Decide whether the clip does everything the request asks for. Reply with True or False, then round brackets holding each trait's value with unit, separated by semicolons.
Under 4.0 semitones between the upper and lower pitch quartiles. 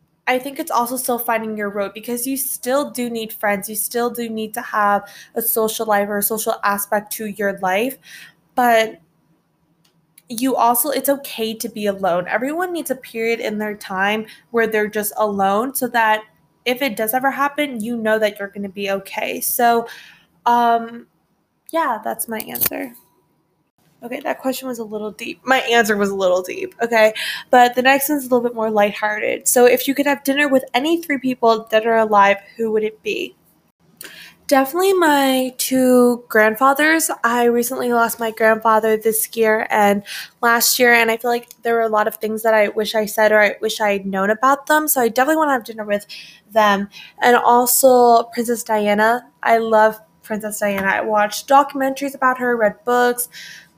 True (3.0 semitones)